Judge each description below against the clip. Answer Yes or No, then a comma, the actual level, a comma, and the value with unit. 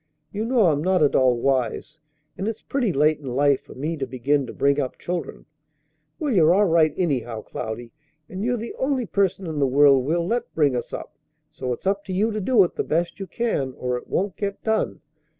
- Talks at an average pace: No, fast, 220 wpm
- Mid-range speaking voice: Yes, medium, 165 Hz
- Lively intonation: Yes, wide, 6.5 semitones